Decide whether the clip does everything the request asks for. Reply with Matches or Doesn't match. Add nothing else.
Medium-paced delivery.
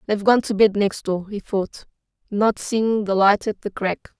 Doesn't match